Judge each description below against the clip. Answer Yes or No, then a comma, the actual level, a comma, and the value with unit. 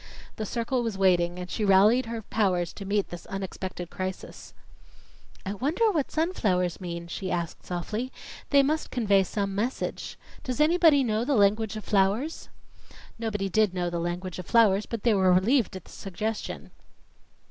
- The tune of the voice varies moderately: Yes, average, 4.0 semitones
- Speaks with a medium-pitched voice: No, high, 205 Hz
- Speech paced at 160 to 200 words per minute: Yes, average, 165 wpm